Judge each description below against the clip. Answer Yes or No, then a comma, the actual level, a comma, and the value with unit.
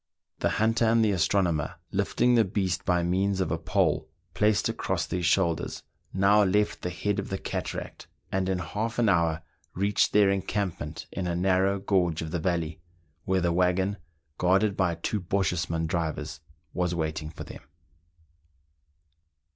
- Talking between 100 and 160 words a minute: Yes, average, 155 wpm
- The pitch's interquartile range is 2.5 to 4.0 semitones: Yes, average, 3.0 semitones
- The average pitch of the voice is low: Yes, very low, 95 Hz